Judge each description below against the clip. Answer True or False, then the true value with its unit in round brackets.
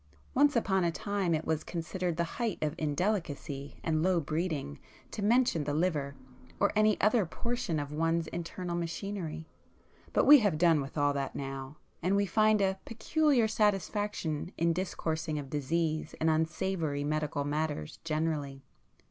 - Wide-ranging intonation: False (4.6 semitones)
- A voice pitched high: False (165 Hz)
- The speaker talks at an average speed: True (150 wpm)